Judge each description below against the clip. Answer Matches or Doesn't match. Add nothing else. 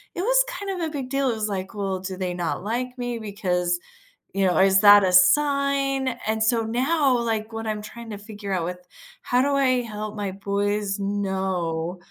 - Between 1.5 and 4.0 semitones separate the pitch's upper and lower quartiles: Doesn't match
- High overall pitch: Matches